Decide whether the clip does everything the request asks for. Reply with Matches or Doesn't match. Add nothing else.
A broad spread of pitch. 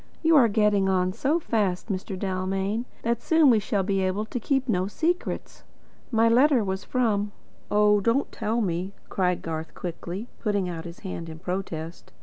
Doesn't match